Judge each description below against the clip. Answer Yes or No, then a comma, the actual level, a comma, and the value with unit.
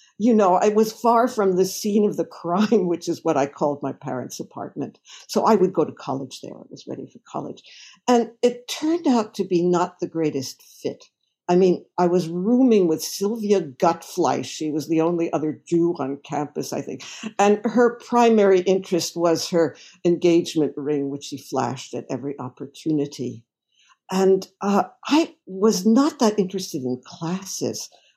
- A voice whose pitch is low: No, medium, 175 Hz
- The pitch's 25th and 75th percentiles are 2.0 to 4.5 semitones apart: No, wide, 5.5 semitones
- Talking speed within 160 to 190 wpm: Yes, average, 175 wpm